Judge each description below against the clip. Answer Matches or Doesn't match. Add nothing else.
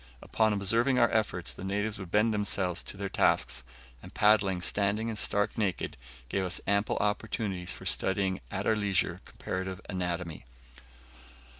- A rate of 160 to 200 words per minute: Doesn't match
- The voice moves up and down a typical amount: Doesn't match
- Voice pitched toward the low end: Matches